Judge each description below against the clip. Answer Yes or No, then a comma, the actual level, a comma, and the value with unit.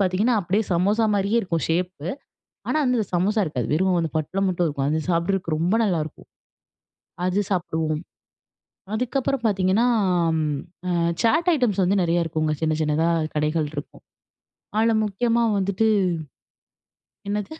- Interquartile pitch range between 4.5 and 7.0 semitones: Yes, average, 4.8 semitones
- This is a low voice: No, medium, 185 Hz